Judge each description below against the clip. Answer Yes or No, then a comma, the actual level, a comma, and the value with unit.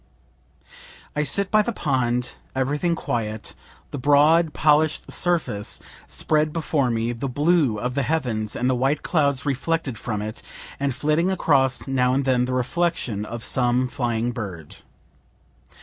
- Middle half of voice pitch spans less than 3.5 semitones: No, average, 4.0 semitones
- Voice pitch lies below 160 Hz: Yes, low, 135 Hz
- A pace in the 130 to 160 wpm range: Yes, average, 150 wpm